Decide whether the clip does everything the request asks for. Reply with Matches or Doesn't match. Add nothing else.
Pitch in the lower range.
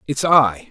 Matches